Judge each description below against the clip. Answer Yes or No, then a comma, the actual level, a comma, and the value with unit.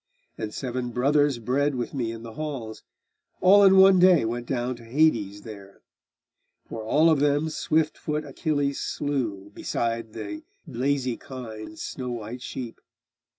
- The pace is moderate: Yes, average, 150 wpm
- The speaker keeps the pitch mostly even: No, average, 4.6 semitones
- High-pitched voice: No, low, 130 Hz